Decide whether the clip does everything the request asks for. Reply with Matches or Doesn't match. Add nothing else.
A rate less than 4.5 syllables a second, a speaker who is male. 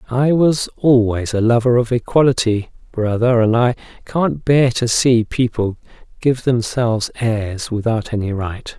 Matches